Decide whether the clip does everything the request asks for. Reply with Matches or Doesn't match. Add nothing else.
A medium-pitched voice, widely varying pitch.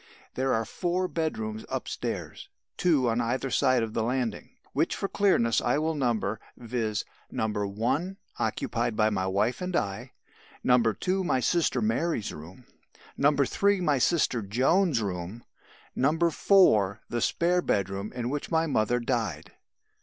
Doesn't match